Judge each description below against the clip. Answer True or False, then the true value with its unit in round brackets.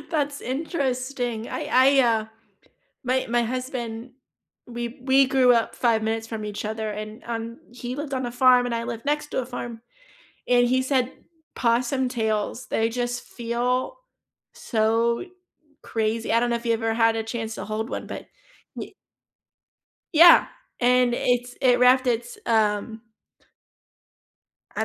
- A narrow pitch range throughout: True (2.1 semitones)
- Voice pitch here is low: False (240 Hz)